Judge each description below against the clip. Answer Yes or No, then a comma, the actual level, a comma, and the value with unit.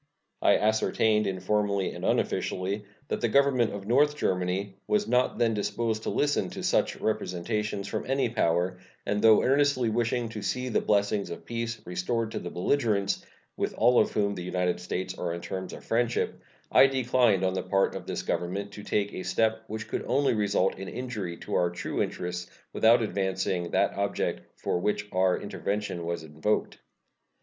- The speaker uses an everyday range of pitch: Yes, average, 4.0 semitones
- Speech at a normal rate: Yes, average, 175 wpm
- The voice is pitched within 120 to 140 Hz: No, low, 105 Hz